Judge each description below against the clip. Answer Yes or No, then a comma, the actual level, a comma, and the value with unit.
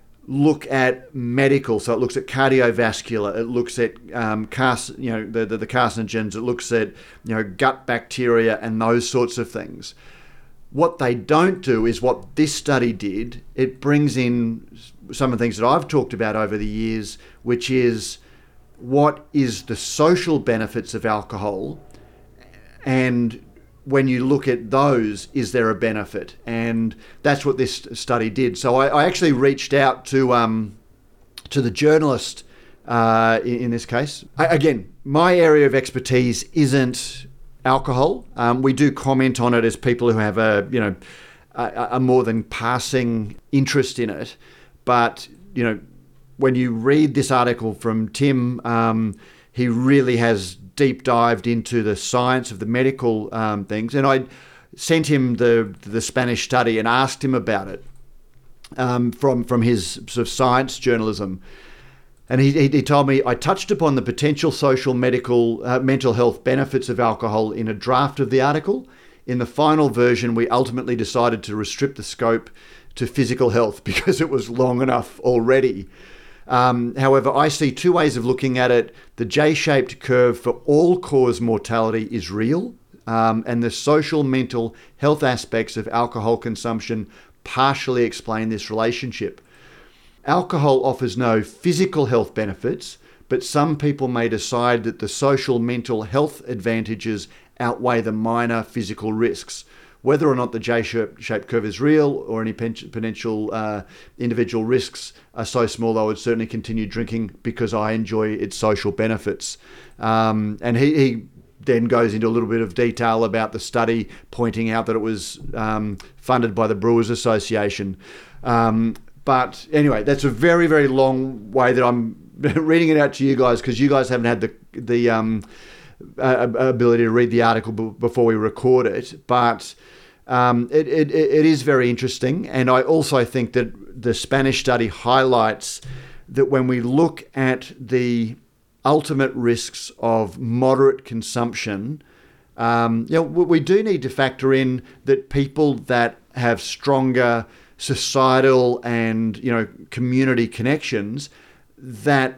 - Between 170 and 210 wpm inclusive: No, average, 160 wpm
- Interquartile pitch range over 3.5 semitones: No, average, 2.8 semitones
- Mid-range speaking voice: No, low, 120 Hz